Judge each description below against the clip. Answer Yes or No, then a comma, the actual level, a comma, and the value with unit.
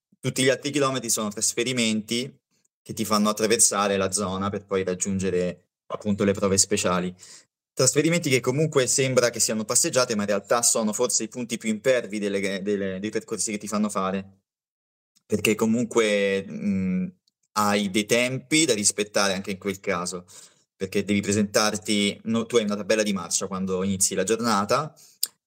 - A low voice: Yes, low, 105 Hz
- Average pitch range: Yes, average, 3.7 semitones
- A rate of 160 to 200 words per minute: Yes, average, 165 wpm